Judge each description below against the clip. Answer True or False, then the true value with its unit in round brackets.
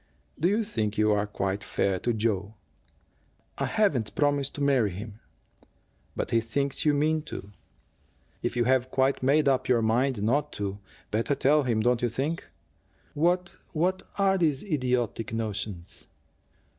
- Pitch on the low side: True (125 Hz)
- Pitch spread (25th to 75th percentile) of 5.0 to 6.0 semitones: True (5.4 semitones)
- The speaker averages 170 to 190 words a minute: False (155 wpm)